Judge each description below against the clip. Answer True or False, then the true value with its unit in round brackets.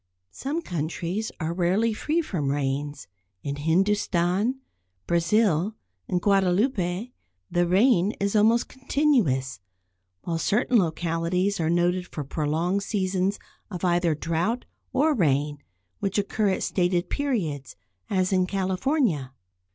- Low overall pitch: False (185 Hz)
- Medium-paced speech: False (115 wpm)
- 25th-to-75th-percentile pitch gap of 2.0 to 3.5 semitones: False (4.2 semitones)